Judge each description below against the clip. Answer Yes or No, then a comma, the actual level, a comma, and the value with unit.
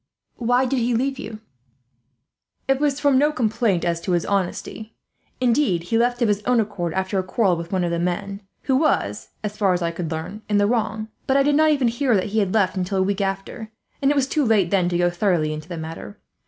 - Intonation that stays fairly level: No, wide, 5.5 semitones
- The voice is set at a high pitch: Yes, high, 205 Hz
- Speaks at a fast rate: Yes, fast, 235 wpm